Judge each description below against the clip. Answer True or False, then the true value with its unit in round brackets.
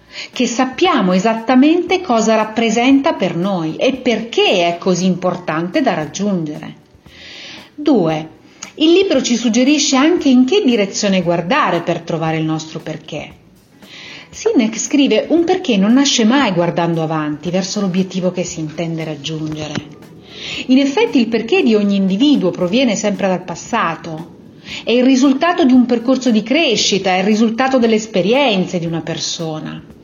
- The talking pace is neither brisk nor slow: True (140 wpm)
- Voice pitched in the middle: False (215 Hz)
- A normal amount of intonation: False (7.4 semitones)